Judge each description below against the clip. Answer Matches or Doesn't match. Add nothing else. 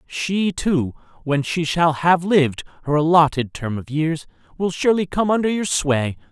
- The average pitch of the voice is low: Doesn't match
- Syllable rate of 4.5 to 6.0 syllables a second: Matches